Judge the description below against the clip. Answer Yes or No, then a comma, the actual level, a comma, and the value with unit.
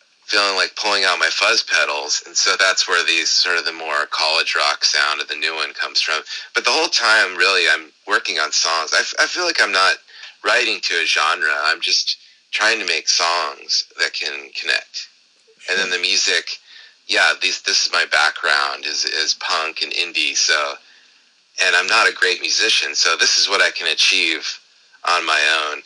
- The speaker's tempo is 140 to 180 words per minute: No, average, 200 wpm